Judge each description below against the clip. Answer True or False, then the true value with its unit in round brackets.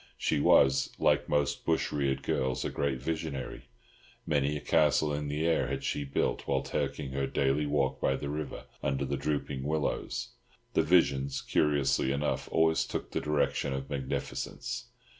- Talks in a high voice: False (70 Hz)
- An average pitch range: False (1.9 semitones)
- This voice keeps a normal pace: True (160 wpm)